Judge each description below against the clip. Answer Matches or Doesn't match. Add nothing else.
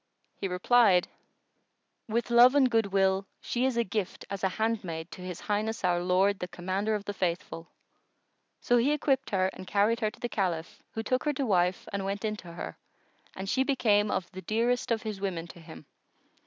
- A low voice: Doesn't match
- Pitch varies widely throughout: Doesn't match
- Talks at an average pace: Matches